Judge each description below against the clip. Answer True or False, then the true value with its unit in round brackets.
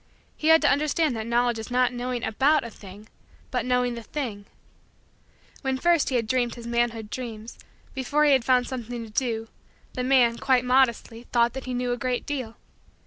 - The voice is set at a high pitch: True (245 Hz)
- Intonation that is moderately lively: False (2.1 semitones)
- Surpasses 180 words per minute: True (195 wpm)